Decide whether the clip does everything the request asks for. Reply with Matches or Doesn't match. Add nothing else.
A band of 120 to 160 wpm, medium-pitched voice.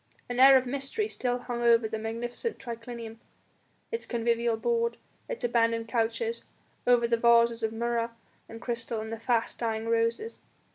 Doesn't match